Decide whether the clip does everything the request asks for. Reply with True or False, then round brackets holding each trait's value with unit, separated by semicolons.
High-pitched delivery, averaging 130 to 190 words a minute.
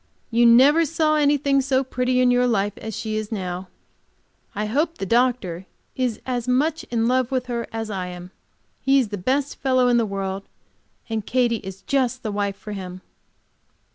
True (240 Hz; 185 wpm)